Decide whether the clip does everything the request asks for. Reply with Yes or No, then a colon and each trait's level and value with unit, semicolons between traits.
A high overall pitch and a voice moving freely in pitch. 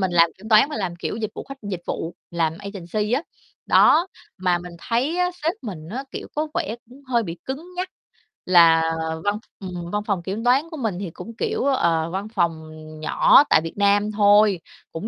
Yes: high, 205 Hz; wide, 5.9 semitones